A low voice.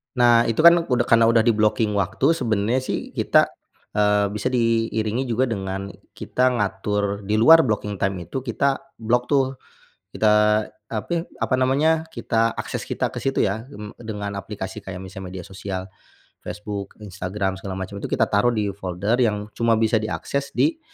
Yes: low, 110 Hz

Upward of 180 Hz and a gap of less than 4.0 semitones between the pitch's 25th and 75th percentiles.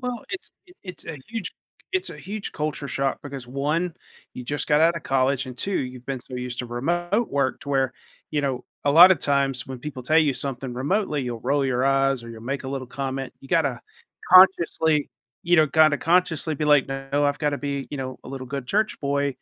No: medium, 140 Hz; average, 3.2 semitones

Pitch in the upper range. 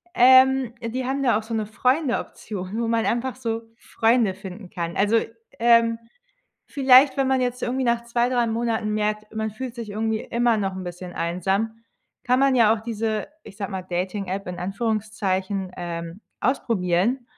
Yes: high, 225 Hz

